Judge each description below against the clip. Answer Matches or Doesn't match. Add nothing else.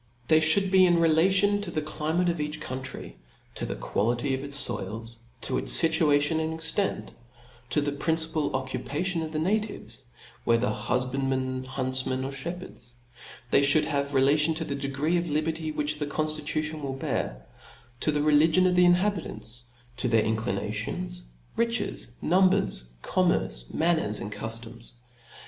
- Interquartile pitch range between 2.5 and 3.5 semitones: Doesn't match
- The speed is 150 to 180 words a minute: Matches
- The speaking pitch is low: Doesn't match